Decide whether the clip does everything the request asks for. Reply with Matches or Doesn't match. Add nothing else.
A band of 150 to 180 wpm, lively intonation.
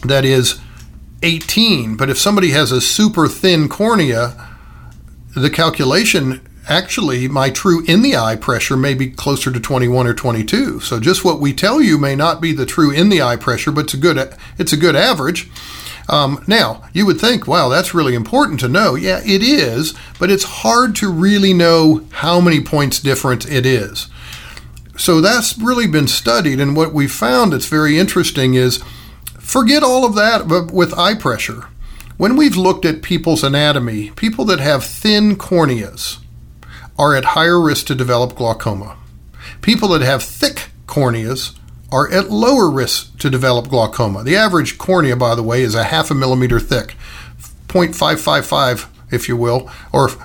Matches